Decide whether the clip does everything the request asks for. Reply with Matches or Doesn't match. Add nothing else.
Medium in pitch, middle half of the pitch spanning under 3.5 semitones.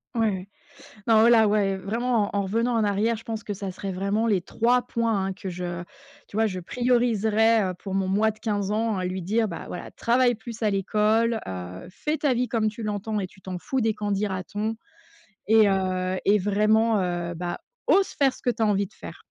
Doesn't match